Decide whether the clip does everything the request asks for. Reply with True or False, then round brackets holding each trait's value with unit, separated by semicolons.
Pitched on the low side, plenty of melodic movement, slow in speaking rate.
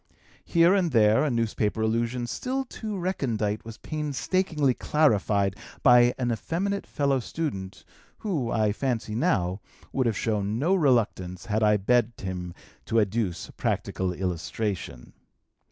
True (115 Hz; 6.1 semitones; 130 wpm)